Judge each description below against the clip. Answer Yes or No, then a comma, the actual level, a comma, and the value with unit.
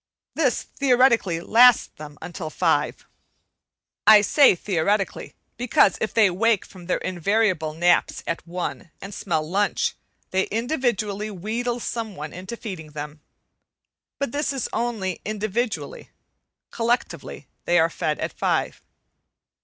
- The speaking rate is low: Yes, slow, 125 wpm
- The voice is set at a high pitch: Yes, high, 200 Hz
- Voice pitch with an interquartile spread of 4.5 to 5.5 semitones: Yes, average, 5.1 semitones